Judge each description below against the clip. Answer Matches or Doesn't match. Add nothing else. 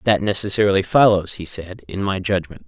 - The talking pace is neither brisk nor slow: Matches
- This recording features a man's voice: Matches